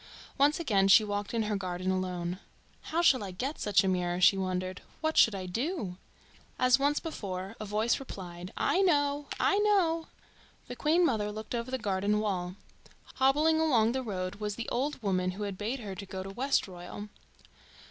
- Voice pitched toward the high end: Yes, high, 210 Hz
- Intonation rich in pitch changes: Yes, wide, 6.5 semitones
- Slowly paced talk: No, average, 180 wpm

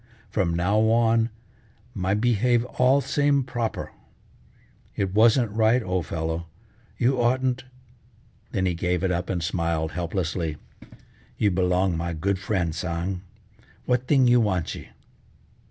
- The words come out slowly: Yes, slow, 130 wpm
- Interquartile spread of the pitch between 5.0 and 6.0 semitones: Yes, average, 5.3 semitones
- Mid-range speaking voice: No, low, 100 Hz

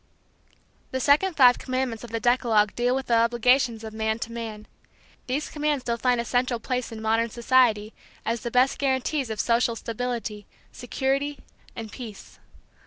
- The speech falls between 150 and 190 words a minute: Yes, average, 165 wpm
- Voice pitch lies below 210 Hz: No, high, 240 Hz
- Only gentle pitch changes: Yes, narrow, 2.3 semitones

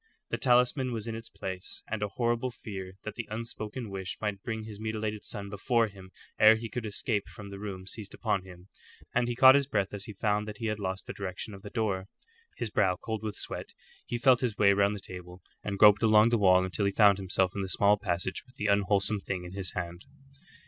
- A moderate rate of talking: No, fast, 230 wpm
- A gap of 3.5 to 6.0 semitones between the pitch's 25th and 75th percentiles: No, narrow, 2.5 semitones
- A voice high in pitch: No, low, 105 Hz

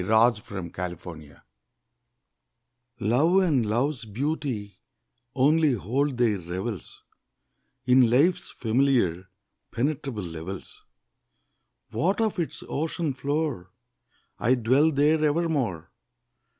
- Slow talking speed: Yes, slow, 90 wpm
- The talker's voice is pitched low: Yes, low, 125 Hz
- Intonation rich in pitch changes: Yes, wide, 6.7 semitones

